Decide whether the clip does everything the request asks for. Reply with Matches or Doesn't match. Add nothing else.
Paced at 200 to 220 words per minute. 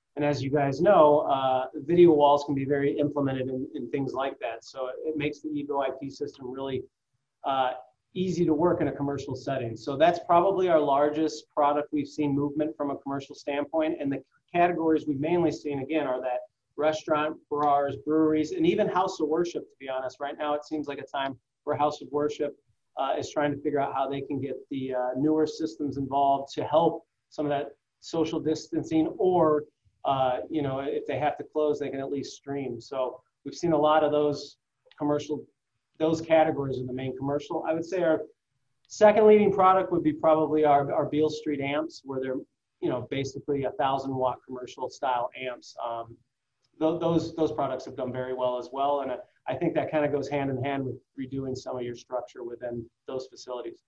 Matches